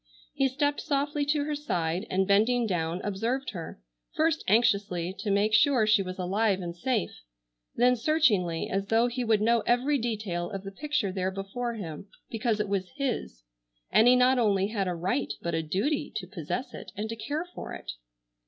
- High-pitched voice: Yes, high, 215 Hz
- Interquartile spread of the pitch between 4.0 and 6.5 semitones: Yes, average, 4.9 semitones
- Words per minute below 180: No, average, 190 wpm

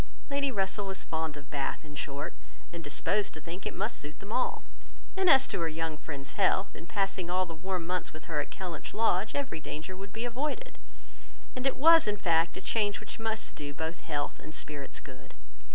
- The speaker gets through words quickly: Yes, fast, 210 wpm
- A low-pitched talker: No, medium, 185 Hz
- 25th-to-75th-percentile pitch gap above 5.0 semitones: Yes, wide, 5.4 semitones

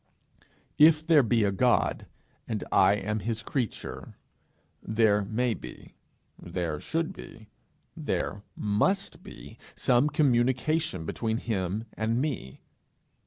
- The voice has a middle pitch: No, low, 115 Hz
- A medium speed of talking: No, slow, 120 wpm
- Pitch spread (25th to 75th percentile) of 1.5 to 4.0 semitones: No, average, 4.6 semitones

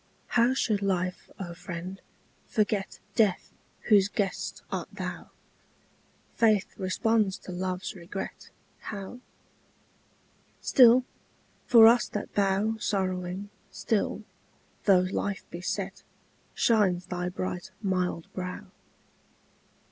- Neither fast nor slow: No, slow, 100 wpm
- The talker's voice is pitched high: Yes, high, 195 Hz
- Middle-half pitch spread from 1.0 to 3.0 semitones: Yes, average, 2.7 semitones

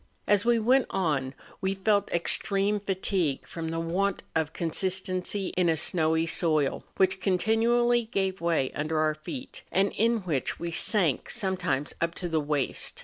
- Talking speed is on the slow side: No, average, 160 wpm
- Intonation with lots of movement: No, average, 3.8 semitones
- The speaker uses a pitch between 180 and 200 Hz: Yes, medium, 185 Hz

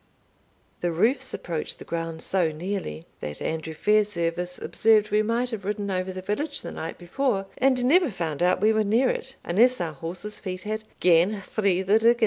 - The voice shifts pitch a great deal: No, average, 4.4 semitones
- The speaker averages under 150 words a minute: No, average, 185 wpm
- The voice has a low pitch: No, high, 200 Hz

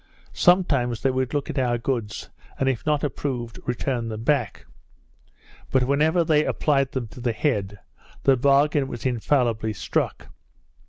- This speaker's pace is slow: No, average, 150 wpm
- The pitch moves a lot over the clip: No, average, 3.4 semitones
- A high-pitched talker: No, low, 130 Hz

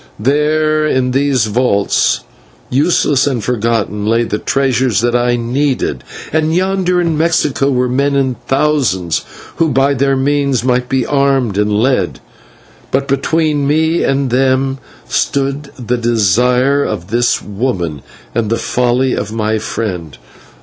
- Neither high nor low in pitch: No, low, 130 Hz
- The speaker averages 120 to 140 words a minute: Yes, slow, 135 wpm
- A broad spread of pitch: No, average, 3.4 semitones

